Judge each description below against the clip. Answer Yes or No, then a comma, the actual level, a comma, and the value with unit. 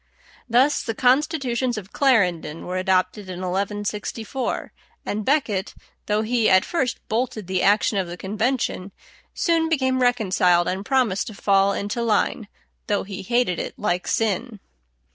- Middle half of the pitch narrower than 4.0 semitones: No, average, 4.6 semitones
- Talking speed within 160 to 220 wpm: No, average, 145 wpm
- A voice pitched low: No, high, 210 Hz